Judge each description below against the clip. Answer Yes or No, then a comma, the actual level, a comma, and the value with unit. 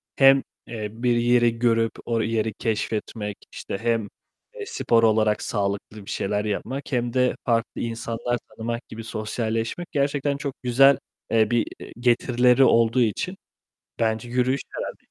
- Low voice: Yes, low, 115 Hz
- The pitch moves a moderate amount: No, narrow, 2.0 semitones